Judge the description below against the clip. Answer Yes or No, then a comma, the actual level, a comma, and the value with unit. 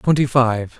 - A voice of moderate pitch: No, low, 125 Hz